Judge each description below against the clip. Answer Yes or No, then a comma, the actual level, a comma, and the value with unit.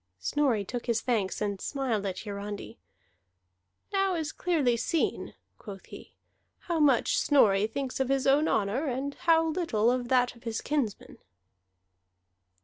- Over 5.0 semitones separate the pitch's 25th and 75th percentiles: Yes, wide, 5.5 semitones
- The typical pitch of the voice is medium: No, very high, 250 Hz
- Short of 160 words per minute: Yes, average, 140 wpm